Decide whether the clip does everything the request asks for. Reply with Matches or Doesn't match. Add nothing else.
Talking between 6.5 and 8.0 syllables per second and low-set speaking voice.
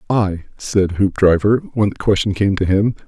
Doesn't match